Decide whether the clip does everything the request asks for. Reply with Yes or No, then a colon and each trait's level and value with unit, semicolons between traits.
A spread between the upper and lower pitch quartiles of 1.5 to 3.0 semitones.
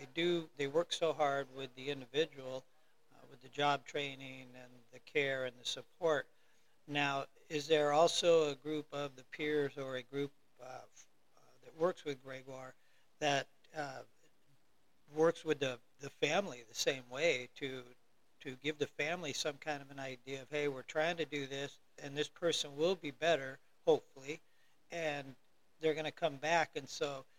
Yes: narrow, 2.5 semitones